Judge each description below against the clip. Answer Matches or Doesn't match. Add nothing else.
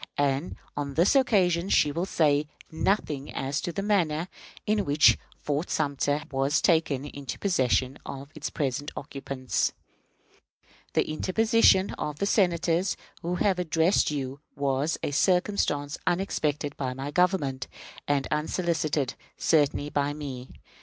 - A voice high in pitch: Doesn't match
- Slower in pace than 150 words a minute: Matches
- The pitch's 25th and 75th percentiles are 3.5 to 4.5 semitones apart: Matches